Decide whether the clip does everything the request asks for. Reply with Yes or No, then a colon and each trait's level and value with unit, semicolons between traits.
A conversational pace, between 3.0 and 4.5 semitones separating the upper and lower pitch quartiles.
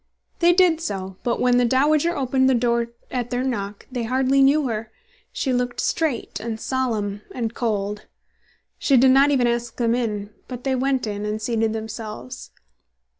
Yes: average, 175 wpm; average, 3.3 semitones